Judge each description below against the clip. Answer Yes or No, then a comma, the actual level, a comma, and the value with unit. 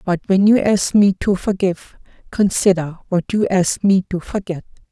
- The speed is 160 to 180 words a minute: Yes, average, 170 wpm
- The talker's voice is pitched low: No, high, 190 Hz